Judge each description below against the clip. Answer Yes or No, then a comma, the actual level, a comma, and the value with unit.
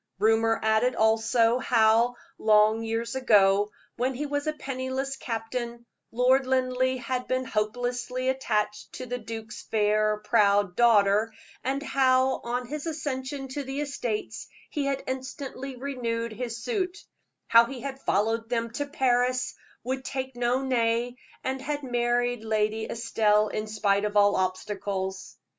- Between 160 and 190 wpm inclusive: No, average, 140 wpm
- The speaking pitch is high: Yes, high, 240 Hz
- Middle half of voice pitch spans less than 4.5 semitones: Yes, average, 3.1 semitones